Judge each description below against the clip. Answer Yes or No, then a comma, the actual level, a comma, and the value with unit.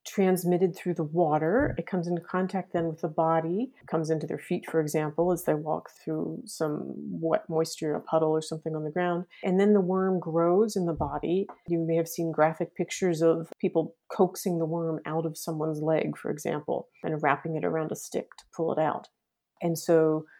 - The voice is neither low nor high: Yes, medium, 165 Hz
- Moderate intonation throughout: No, narrow, 2.1 semitones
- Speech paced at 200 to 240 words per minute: Yes, fast, 205 wpm